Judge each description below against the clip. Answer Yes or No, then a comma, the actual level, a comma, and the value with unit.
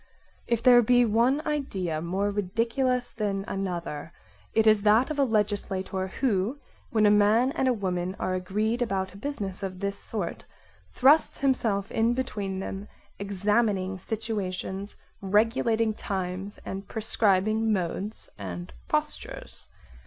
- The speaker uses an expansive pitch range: No, average, 3.2 semitones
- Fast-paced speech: No, slow, 135 wpm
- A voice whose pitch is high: Yes, high, 205 Hz